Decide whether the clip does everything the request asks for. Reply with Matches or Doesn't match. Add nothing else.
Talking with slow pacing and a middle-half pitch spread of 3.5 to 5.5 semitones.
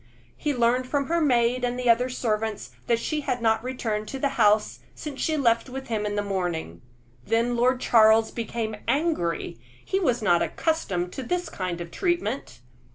Doesn't match